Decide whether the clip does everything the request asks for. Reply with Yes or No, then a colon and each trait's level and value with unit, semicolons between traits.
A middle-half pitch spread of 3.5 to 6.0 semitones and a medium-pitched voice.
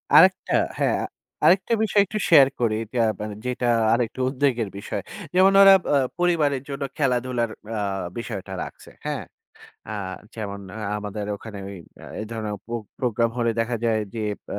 No: average, 4.5 semitones; low, 120 Hz